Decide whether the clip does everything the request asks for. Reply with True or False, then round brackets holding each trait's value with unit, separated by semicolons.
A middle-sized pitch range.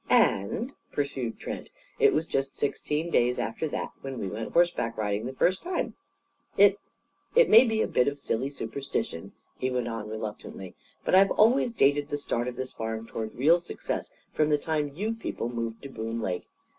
False (5.9 semitones)